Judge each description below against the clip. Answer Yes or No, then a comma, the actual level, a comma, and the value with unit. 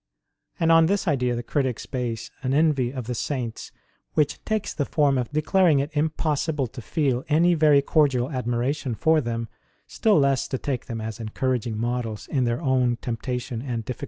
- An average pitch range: Yes, average, 3.9 semitones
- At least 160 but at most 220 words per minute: Yes, average, 180 wpm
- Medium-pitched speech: No, low, 130 Hz